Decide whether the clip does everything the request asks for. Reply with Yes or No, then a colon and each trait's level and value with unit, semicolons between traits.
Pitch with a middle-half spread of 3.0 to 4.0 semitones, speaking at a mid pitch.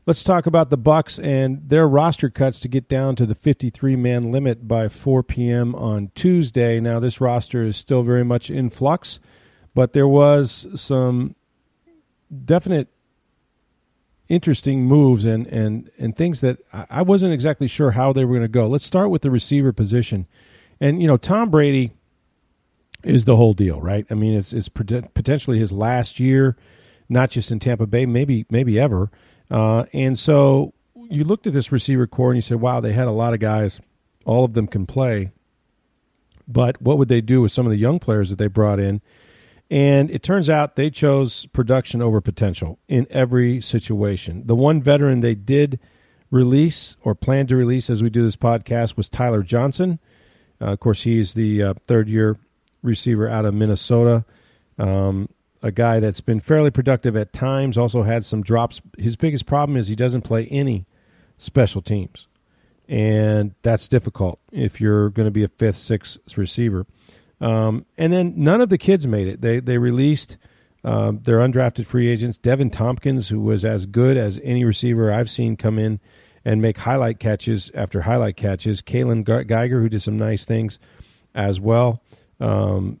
No: average, 3.6 semitones; low, 120 Hz